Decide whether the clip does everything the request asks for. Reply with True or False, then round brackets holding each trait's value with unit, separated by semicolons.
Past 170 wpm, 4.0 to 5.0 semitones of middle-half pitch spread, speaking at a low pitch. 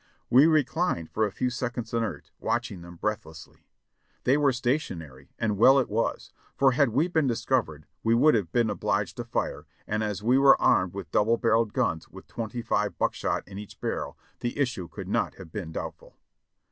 True (185 wpm; 4.3 semitones; 115 Hz)